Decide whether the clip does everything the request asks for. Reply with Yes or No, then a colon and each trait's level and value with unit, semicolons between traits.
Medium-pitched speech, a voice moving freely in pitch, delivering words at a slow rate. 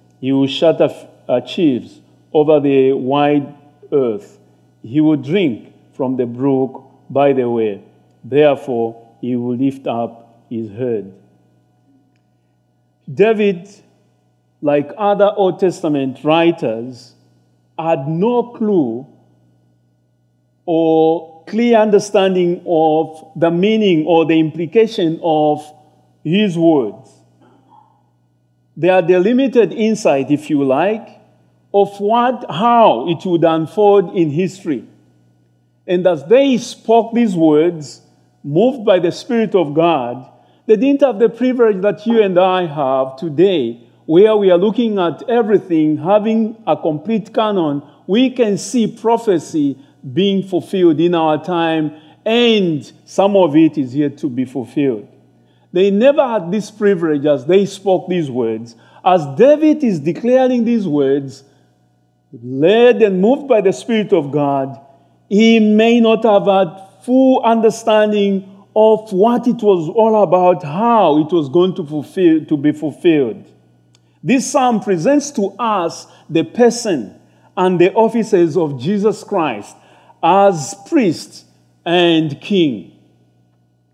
Yes: medium, 165 Hz; wide, 7.7 semitones; slow, 125 wpm